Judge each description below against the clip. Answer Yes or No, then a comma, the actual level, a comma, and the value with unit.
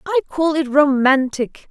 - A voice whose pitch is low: No, very high, 290 Hz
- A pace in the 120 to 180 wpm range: Yes, average, 140 wpm